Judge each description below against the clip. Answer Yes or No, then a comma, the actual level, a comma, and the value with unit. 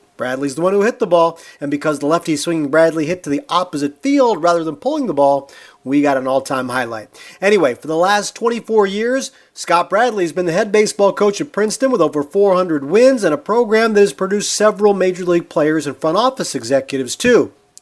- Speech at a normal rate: No, fast, 215 wpm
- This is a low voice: No, medium, 175 Hz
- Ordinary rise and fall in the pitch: No, wide, 6.1 semitones